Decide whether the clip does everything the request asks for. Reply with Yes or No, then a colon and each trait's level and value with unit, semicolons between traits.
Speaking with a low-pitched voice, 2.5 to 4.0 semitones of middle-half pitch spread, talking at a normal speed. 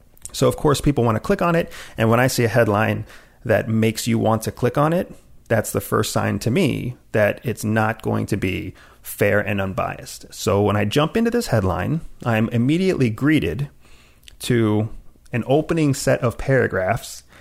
No: low, 115 Hz; average, 4.6 semitones; average, 185 wpm